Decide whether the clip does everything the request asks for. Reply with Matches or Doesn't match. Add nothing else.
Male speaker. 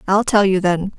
Doesn't match